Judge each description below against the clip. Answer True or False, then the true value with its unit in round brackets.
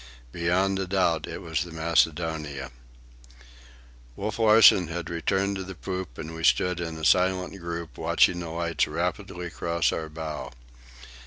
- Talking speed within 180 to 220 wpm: False (150 wpm)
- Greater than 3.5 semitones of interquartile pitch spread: False (2.4 semitones)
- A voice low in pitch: True (85 Hz)